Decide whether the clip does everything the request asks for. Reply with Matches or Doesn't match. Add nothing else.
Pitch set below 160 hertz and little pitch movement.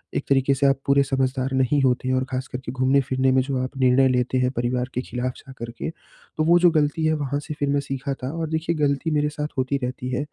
Matches